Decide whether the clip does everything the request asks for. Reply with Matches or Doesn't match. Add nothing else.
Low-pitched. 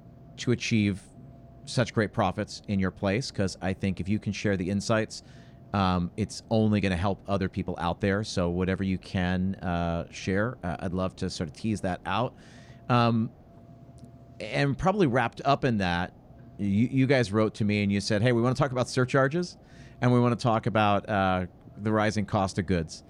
Matches